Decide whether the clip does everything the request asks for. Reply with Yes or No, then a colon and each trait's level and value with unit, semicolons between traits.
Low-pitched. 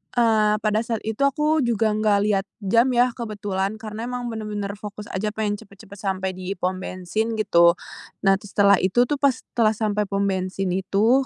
No: high, 210 Hz